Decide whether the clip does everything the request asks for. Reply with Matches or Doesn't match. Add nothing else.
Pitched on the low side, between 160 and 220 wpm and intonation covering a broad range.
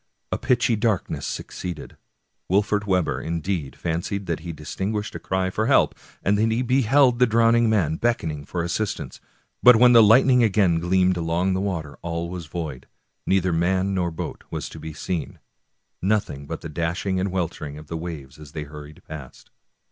Doesn't match